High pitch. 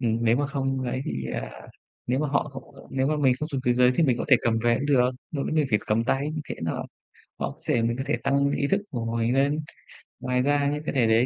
No: low, 130 Hz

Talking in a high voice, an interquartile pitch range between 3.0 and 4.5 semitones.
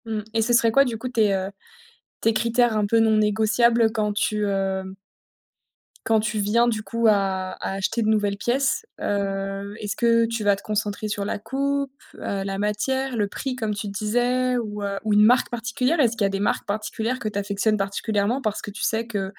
No: high, 215 Hz; narrow, 2.6 semitones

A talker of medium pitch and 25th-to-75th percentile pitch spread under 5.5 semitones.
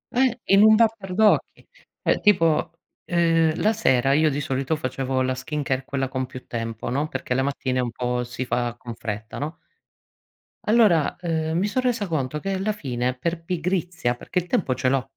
No: medium, 150 Hz; wide, 6.0 semitones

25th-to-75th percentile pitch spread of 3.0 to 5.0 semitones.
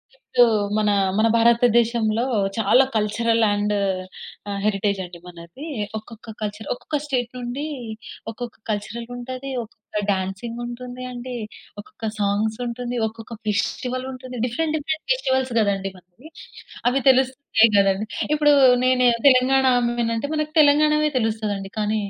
Yes: average, 3.3 semitones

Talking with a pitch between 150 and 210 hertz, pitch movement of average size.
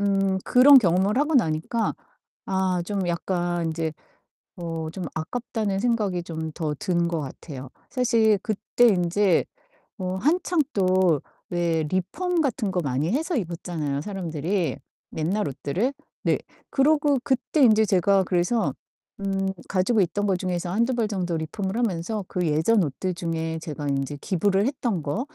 Yes: medium, 185 Hz; average, 4.8 semitones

